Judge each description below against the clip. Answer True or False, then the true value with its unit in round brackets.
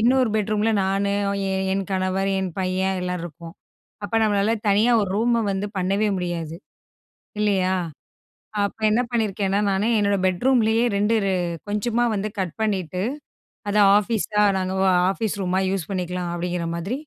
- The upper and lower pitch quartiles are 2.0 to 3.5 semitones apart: True (2.5 semitones)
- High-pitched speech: True (195 Hz)